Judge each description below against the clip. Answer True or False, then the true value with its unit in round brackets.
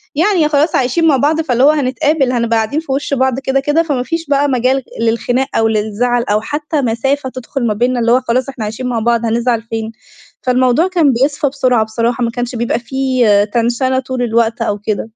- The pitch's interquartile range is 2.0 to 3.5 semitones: True (2.9 semitones)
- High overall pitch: True (255 Hz)